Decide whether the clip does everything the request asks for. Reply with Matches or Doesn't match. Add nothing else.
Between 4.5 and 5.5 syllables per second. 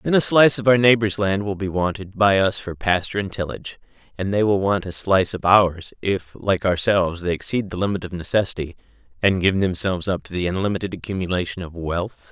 Doesn't match